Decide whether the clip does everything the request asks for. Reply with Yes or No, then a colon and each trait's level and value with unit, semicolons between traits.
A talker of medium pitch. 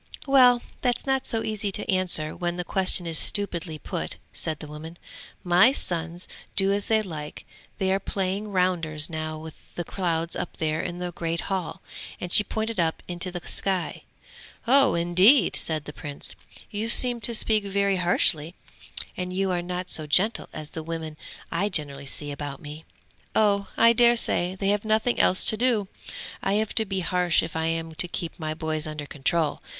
Yes: medium, 180 Hz